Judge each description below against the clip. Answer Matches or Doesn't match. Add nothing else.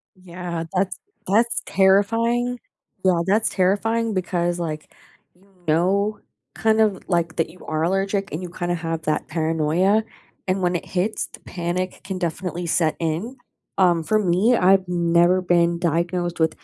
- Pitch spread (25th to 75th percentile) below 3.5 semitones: Matches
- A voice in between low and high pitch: Matches